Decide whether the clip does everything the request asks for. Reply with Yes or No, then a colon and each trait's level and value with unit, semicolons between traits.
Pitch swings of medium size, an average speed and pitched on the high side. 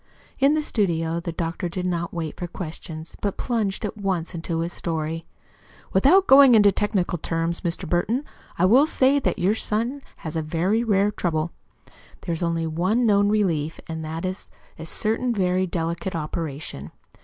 No: average, 4.2 semitones; average, 170 wpm; medium, 180 Hz